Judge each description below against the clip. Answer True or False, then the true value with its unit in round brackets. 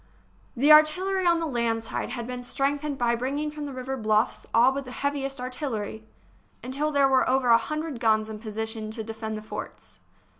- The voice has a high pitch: True (255 Hz)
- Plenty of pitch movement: False (4.2 semitones)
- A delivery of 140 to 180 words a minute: False (195 wpm)